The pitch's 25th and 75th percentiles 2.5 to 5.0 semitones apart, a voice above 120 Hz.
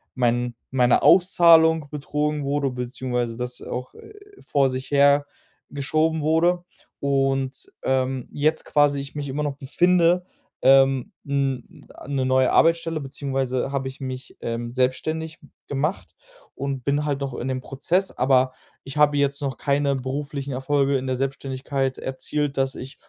No: narrow, 2.1 semitones; medium, 140 Hz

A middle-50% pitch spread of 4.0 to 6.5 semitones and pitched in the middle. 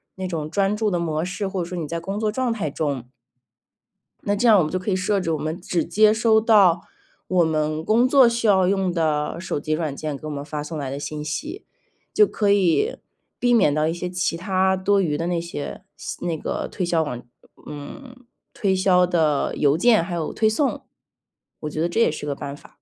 Yes: average, 4.8 semitones; medium, 175 Hz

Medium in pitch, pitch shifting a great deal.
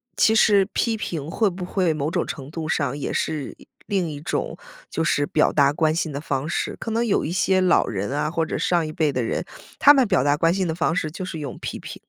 No: medium, 160 Hz; average, 4.2 semitones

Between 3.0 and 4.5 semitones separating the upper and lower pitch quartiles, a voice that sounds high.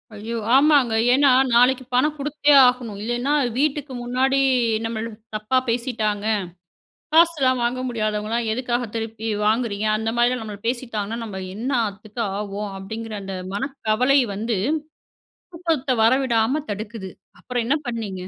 Yes: average, 3.3 semitones; high, 235 Hz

